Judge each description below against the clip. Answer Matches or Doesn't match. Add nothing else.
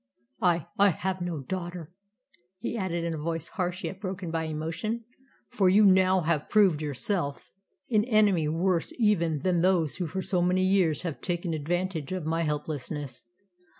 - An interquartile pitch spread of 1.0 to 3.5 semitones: Matches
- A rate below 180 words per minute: Matches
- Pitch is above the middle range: Doesn't match